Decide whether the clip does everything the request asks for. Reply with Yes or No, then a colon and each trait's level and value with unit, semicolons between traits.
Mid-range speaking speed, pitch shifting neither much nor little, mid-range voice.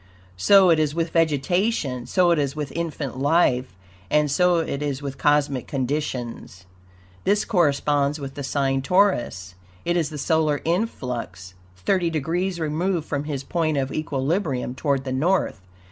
Yes: average, 150 wpm; average, 3.9 semitones; medium, 150 Hz